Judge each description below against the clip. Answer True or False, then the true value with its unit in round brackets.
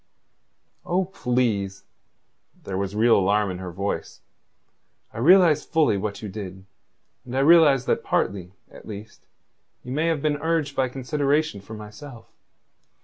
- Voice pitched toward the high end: False (120 Hz)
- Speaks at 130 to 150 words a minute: True (145 wpm)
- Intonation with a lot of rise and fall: True (6.8 semitones)